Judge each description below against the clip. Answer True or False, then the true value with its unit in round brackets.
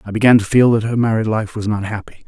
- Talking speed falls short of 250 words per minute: False (290 wpm)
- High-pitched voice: False (110 Hz)